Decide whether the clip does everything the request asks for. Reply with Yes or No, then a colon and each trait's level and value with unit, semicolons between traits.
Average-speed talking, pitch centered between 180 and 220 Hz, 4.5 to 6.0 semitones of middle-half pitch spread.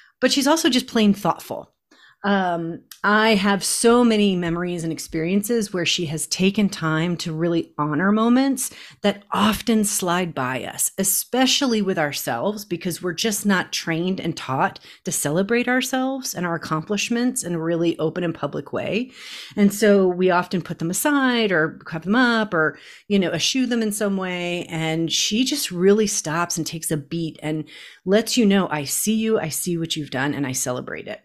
Yes: average, 180 wpm; medium, 185 Hz; average, 4.8 semitones